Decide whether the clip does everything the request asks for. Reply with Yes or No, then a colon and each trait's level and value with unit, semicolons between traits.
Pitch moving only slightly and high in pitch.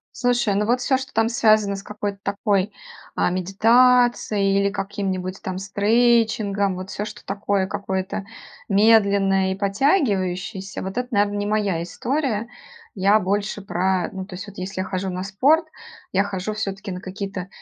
Yes: narrow, 2.1 semitones; high, 200 Hz